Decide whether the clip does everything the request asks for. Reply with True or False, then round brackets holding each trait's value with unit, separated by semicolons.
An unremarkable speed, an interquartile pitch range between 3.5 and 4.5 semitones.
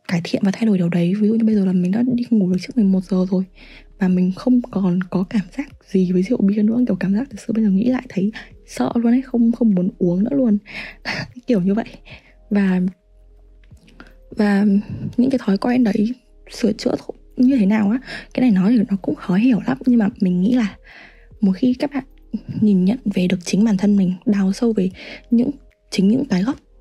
True (230 wpm; 4.0 semitones)